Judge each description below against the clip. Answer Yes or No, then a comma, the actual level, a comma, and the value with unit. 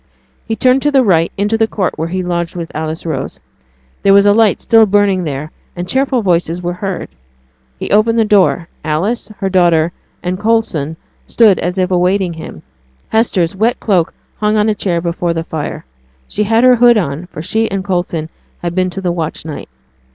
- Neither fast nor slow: Yes, average, 195 wpm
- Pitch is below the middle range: No, medium, 185 Hz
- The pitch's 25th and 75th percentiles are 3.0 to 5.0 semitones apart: Yes, average, 4.1 semitones